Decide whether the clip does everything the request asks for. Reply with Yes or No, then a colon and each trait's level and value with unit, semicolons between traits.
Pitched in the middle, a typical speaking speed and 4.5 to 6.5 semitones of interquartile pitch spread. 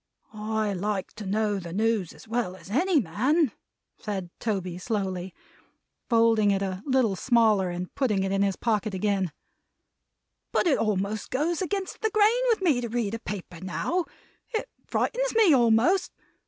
No: high, 215 Hz; average, 160 wpm; wide, 5.5 semitones